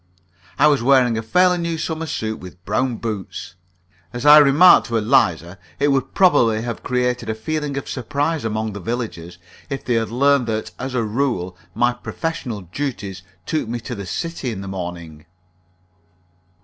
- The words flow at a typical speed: Yes, average, 170 wpm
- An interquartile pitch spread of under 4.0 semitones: No, average, 5.0 semitones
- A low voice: Yes, low, 120 Hz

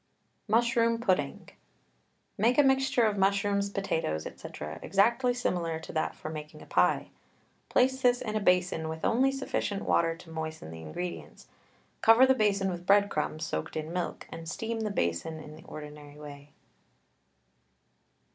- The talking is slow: No, average, 155 wpm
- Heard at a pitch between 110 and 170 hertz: No, medium, 185 Hz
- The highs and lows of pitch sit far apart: Yes, wide, 6.3 semitones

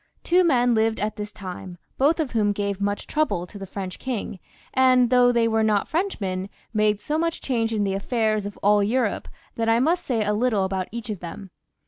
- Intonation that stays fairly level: No, average, 3.7 semitones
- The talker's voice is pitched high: Yes, high, 220 Hz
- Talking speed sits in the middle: No, fast, 210 wpm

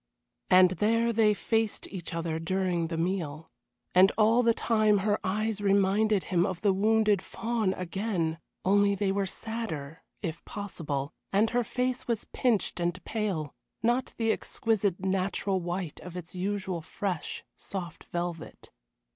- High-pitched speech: Yes, high, 195 Hz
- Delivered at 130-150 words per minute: Yes, average, 145 wpm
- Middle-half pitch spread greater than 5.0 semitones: No, average, 3.7 semitones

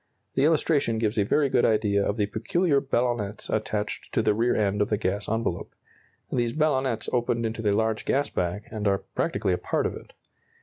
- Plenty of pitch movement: No, average, 3.3 semitones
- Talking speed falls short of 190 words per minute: No, average, 200 wpm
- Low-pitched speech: Yes, low, 110 Hz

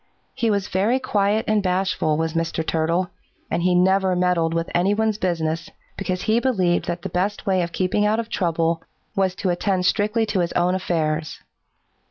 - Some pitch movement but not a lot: Yes, average, 3.1 semitones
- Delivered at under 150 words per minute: No, average, 185 wpm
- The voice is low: No, medium, 185 Hz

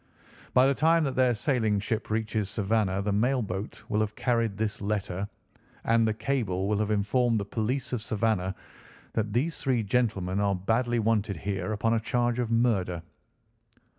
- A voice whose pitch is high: No, low, 110 Hz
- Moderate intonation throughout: Yes, average, 3.1 semitones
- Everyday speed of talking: Yes, average, 170 wpm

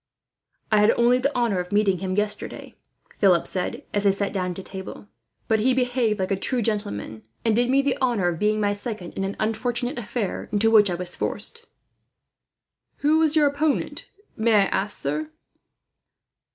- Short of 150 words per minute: No, average, 180 wpm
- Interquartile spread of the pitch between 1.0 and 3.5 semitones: No, average, 4.2 semitones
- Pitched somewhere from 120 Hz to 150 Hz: No, high, 210 Hz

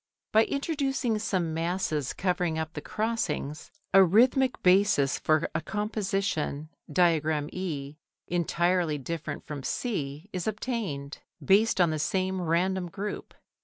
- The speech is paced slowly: Yes, slow, 125 wpm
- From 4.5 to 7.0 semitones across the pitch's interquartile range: Yes, average, 5.0 semitones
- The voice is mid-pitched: Yes, medium, 180 Hz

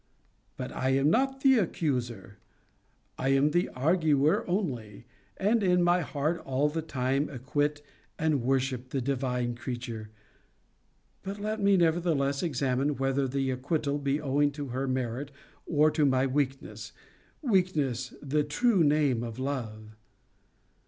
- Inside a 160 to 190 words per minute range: No, slow, 135 wpm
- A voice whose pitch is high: No, medium, 140 Hz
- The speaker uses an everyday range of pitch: Yes, average, 3.7 semitones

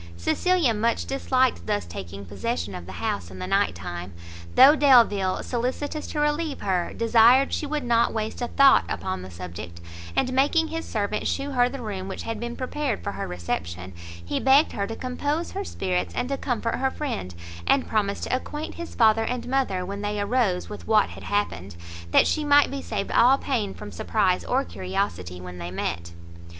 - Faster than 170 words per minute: Yes, average, 190 wpm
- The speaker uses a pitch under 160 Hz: No, high, 220 Hz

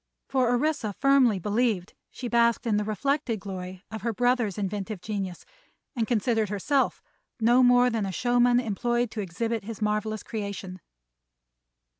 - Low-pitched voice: No, high, 225 Hz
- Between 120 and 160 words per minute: Yes, average, 145 wpm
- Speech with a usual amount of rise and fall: Yes, average, 3.2 semitones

